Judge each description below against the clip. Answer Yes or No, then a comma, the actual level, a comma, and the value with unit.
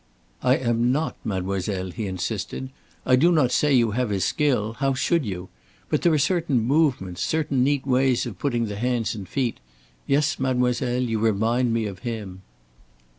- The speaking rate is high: No, average, 175 wpm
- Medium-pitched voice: No, low, 120 Hz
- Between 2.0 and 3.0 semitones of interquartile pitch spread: No, average, 4.2 semitones